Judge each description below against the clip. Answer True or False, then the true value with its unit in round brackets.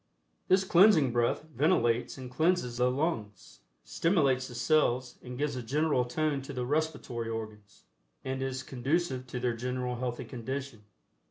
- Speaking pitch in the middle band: False (130 Hz)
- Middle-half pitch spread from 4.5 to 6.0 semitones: False (3.6 semitones)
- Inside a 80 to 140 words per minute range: False (150 wpm)